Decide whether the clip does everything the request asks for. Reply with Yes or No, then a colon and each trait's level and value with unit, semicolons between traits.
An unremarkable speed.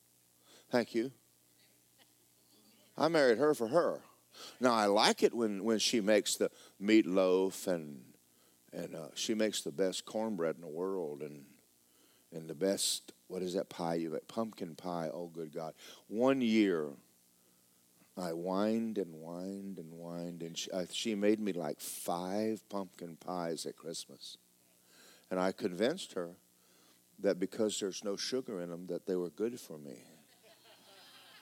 Yes: average, 155 wpm